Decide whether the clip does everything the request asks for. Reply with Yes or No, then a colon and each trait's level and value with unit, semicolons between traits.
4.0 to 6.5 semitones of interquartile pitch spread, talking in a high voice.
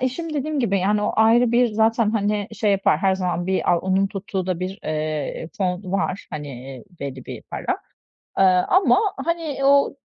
Yes: average, 4.3 semitones; high, 195 Hz